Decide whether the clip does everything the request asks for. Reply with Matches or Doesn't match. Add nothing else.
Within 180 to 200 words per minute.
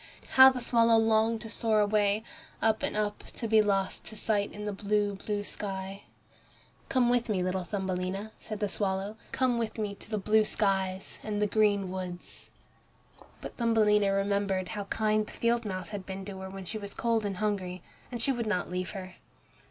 Matches